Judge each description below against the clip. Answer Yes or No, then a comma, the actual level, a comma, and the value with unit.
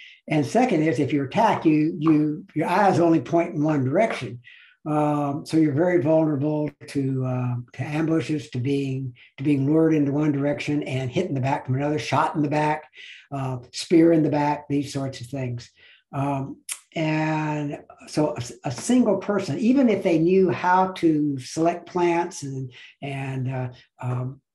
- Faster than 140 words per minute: Yes, average, 175 wpm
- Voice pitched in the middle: Yes, medium, 150 Hz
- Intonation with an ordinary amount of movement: Yes, average, 3.2 semitones